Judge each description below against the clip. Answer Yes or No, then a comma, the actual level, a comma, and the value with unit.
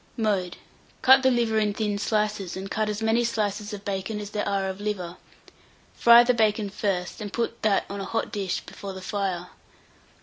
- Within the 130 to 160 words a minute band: No, average, 195 wpm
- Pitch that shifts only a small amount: Yes, narrow, 2.1 semitones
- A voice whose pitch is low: No, high, 210 Hz